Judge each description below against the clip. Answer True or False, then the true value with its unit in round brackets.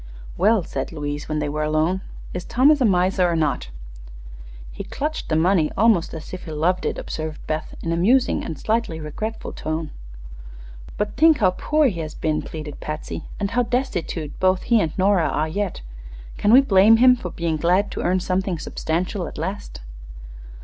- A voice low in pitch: False (180 Hz)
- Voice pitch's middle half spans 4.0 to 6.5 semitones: True (4.9 semitones)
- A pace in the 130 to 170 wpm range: False (185 wpm)